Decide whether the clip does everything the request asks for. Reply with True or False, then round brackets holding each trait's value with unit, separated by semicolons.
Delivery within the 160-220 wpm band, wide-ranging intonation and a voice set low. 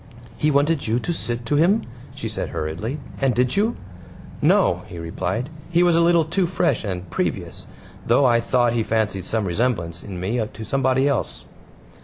True (180 wpm; 6.1 semitones; 120 Hz)